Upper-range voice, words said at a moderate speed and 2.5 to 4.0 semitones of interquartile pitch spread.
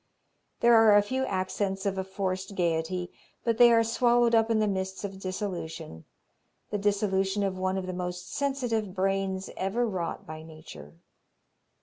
Yes: high, 195 Hz; average, 160 wpm; average, 2.8 semitones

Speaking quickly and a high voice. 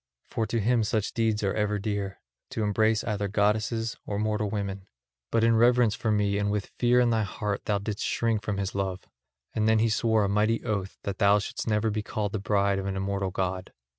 No: fast, 220 wpm; low, 105 Hz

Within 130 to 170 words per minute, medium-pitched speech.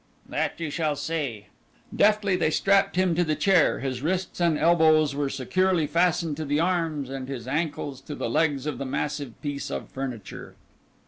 No: average, 180 wpm; medium, 155 Hz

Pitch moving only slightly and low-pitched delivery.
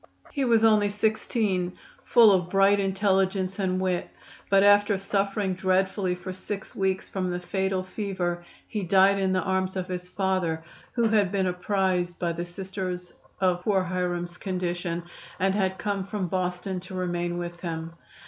No: narrow, 1.7 semitones; high, 190 Hz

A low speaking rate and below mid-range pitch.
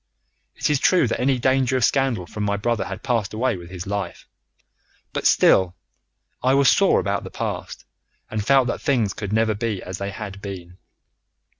No: average, 185 wpm; low, 110 Hz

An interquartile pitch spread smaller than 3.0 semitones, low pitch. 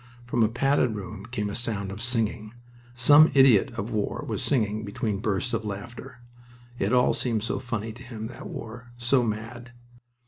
Yes: narrow, 2.5 semitones; low, 115 Hz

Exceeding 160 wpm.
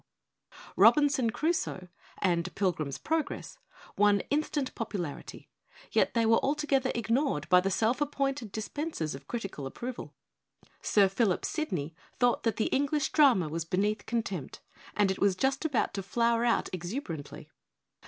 No: average, 145 wpm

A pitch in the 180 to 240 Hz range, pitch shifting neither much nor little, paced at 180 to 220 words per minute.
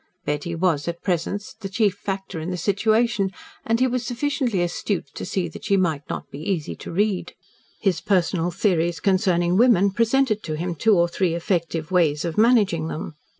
Yes: medium, 185 Hz; average, 3.8 semitones; average, 185 wpm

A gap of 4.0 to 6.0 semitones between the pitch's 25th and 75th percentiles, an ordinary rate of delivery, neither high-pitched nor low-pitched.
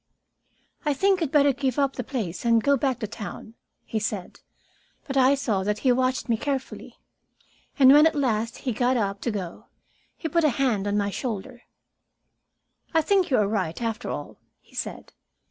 No: average, 4.7 semitones; average, 185 wpm; very high, 250 Hz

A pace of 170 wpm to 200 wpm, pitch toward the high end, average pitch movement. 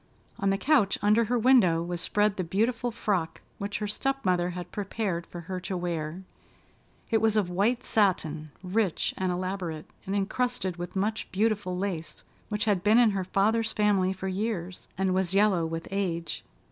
Yes: average, 175 wpm; high, 195 Hz; average, 3.1 semitones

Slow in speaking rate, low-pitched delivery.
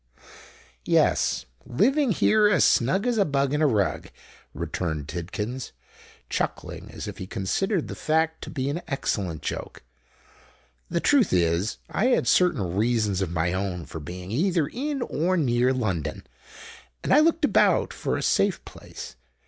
No: average, 150 wpm; low, 130 Hz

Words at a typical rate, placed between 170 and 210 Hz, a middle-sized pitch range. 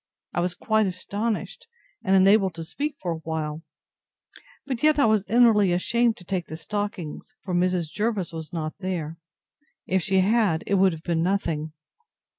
Yes: average, 170 wpm; high, 190 Hz; average, 4.4 semitones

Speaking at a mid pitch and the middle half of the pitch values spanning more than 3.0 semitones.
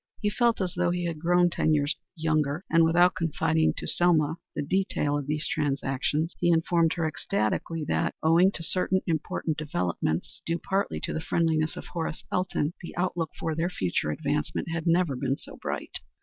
No: medium, 165 Hz; narrow, 2.6 semitones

